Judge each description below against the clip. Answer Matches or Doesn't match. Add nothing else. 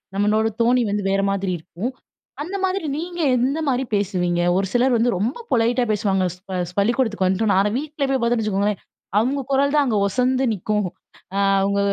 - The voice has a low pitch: Doesn't match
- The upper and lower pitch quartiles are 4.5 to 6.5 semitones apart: Matches